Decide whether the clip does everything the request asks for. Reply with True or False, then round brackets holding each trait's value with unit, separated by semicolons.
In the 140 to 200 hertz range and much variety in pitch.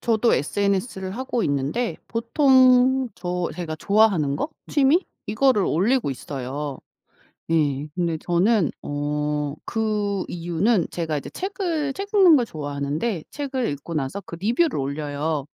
True (190 Hz; 8.6 semitones)